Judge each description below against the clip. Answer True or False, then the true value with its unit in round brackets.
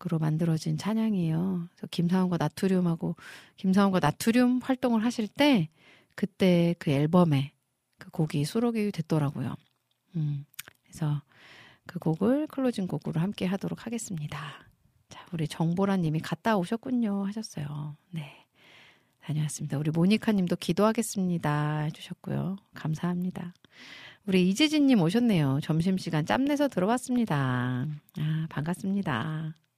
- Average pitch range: True (4.9 semitones)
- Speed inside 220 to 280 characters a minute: False (310 characters per minute)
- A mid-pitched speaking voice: True (175 Hz)